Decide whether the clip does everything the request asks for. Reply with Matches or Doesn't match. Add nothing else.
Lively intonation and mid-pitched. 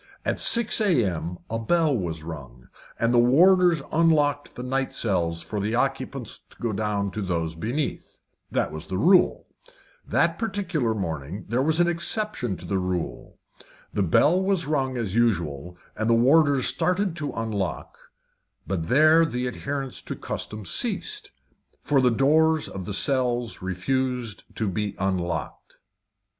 Doesn't match